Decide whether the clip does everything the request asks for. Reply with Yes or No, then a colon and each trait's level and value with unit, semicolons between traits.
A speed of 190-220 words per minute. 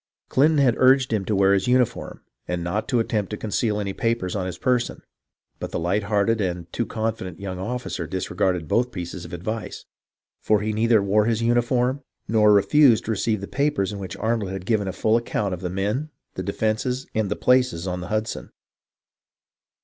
Yes: average, 200 wpm